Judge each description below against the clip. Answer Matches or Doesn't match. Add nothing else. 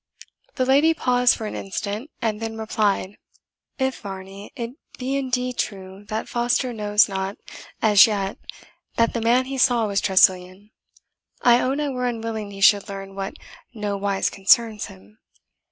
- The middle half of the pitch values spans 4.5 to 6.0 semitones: Doesn't match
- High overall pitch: Matches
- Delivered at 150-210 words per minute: Matches